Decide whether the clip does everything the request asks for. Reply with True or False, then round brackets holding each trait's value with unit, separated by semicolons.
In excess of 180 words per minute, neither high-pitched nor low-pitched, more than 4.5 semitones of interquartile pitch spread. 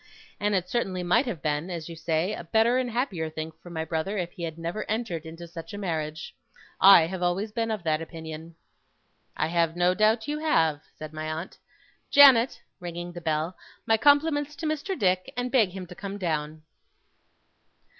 True (190 wpm; 180 Hz; 5.3 semitones)